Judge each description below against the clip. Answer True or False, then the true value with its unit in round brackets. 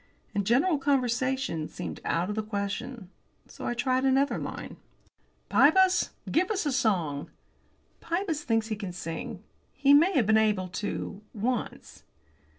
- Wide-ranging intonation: True (5.7 semitones)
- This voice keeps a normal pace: True (145 wpm)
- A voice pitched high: True (240 Hz)